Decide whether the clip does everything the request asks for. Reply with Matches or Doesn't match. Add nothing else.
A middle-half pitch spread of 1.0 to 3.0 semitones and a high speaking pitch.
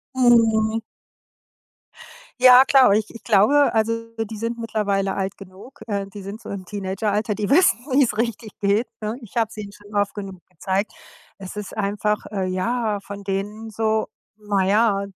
Matches